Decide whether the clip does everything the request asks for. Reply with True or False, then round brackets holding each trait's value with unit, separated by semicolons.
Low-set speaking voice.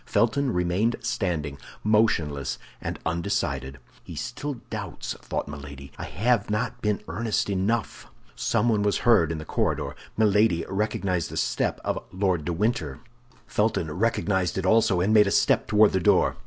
True (100 Hz)